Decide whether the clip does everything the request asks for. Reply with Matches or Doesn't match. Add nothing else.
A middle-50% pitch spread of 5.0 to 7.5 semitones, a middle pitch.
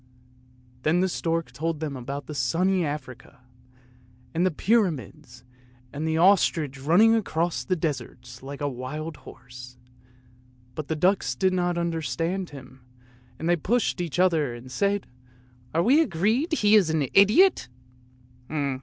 Matches